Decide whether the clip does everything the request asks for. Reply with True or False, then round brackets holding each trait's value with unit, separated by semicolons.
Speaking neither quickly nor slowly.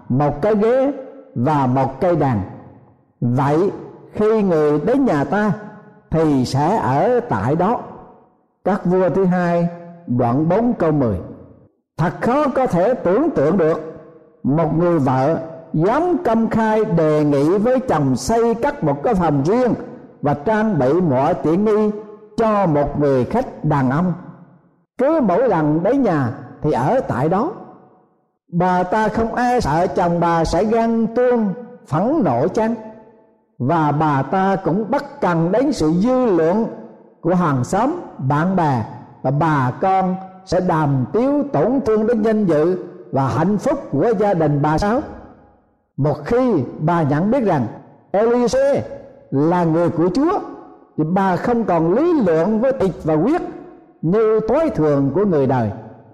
False (155 wpm)